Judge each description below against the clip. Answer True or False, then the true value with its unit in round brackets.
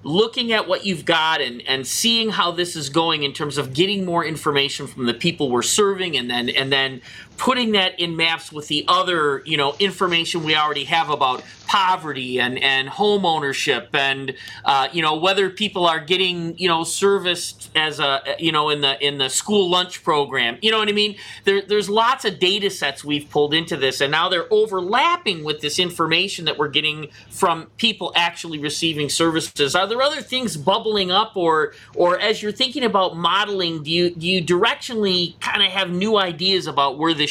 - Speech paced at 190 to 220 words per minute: True (200 wpm)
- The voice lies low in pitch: False (170 Hz)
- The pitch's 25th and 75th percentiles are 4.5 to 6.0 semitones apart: True (4.8 semitones)